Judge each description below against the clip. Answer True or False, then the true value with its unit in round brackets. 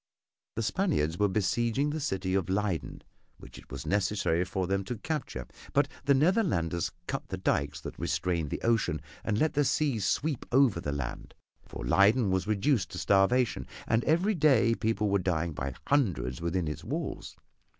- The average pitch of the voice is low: True (100 Hz)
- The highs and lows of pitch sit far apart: True (6.9 semitones)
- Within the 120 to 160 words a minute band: False (170 wpm)